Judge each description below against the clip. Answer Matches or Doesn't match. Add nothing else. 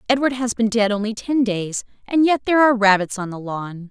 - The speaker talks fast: Matches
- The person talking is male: Doesn't match